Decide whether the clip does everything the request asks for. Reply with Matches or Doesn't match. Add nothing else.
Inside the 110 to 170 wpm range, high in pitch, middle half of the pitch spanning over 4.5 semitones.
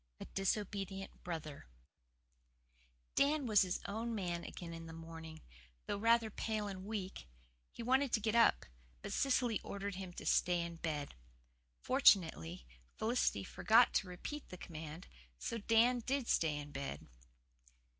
Matches